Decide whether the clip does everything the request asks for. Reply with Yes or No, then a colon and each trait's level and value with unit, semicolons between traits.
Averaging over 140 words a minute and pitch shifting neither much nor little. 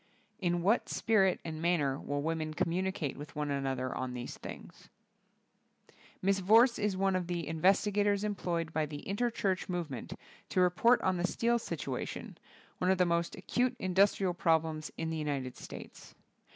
Yes: average, 165 wpm; average, 3.9 semitones